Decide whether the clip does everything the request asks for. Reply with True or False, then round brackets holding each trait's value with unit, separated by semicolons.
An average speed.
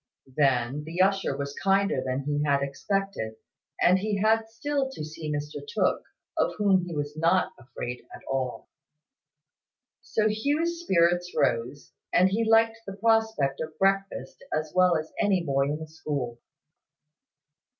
True (150 wpm)